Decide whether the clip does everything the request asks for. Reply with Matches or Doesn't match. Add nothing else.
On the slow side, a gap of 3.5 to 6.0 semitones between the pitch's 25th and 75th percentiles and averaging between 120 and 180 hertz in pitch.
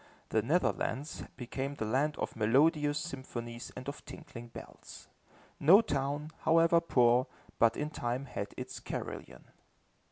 Matches